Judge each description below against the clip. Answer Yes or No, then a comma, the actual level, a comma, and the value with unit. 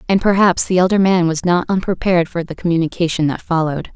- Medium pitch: Yes, medium, 175 Hz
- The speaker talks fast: No, average, 195 wpm